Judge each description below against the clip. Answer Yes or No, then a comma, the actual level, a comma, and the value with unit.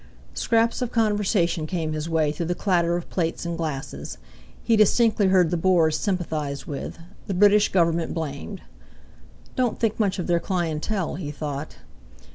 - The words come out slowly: No, average, 155 wpm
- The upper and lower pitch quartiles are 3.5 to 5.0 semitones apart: Yes, average, 4.4 semitones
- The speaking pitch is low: No, medium, 175 Hz